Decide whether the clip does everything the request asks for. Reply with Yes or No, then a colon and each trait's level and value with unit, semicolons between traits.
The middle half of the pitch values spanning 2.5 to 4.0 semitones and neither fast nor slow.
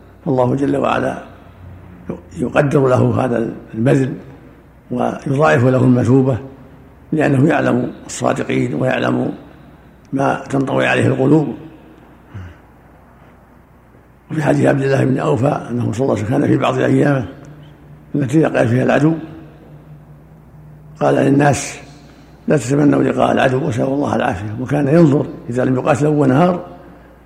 Yes: average, 3.4 semitones; average, 115 wpm